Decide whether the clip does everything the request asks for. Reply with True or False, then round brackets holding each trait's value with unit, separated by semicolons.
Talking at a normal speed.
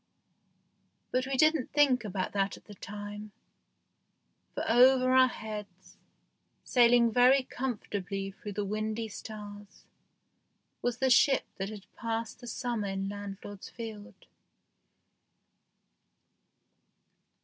False (105 wpm)